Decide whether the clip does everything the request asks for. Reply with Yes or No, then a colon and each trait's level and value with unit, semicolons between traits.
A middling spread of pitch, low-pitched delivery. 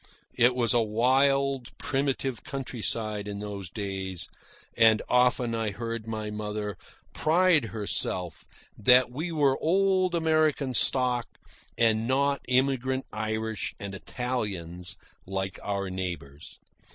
Yes: average, 4.5 semitones; low, 115 Hz